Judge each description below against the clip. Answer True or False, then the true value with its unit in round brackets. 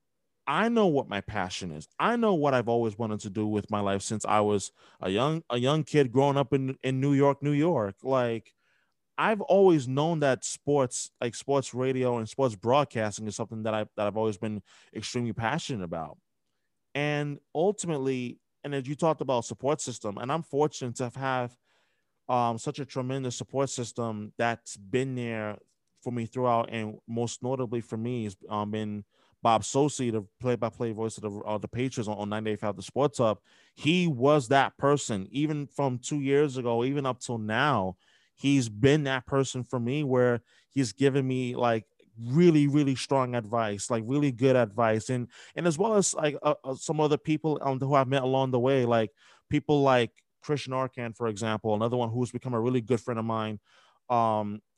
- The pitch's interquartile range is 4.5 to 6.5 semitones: False (3.8 semitones)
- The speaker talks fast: False (190 wpm)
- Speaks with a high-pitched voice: False (125 Hz)